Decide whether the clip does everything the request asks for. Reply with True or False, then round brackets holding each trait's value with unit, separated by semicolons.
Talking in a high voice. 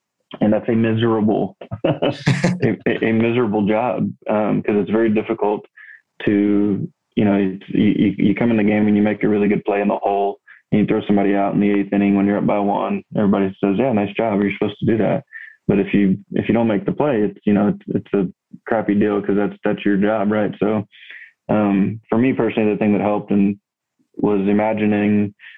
False (105 Hz)